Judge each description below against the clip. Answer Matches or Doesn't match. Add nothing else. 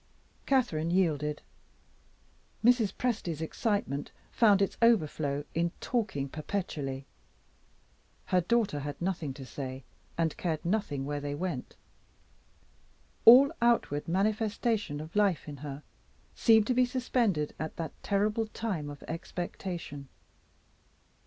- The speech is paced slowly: Matches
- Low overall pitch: Doesn't match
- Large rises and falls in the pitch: Matches